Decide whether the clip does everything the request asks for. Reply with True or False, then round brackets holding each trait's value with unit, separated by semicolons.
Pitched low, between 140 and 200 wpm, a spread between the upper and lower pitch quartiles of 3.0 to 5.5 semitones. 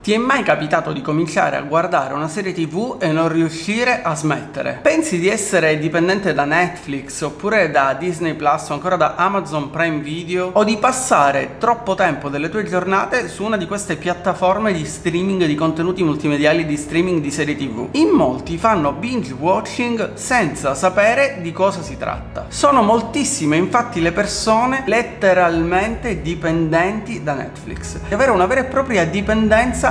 False (180 Hz; 165 wpm; 5.1 semitones)